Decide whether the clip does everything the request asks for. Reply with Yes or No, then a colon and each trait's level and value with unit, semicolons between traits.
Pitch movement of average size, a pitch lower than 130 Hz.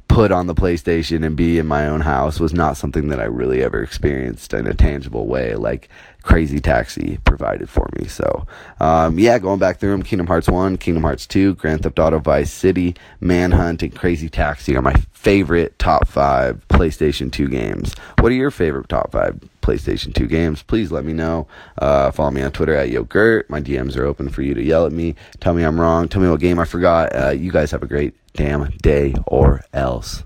Yes: average, 3.3 semitones; very low, 80 Hz